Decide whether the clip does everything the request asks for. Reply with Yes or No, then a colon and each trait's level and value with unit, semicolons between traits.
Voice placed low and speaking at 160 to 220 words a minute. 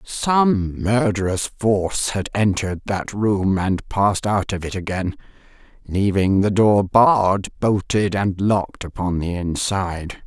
No: low, 100 Hz; slow, 135 wpm